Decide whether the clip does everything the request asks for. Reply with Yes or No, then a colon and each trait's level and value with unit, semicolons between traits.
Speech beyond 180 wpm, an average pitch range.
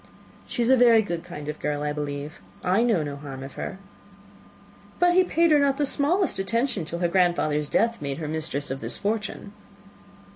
No: average, 195 wpm; wide, 8.3 semitones